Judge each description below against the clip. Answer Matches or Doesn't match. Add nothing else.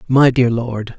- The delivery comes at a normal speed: Matches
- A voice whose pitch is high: Doesn't match